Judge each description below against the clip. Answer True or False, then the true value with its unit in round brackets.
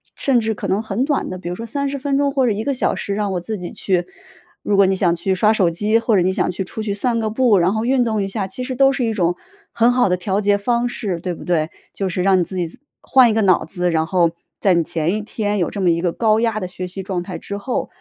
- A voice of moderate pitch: False (200 Hz)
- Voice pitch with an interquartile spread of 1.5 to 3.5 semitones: False (4.1 semitones)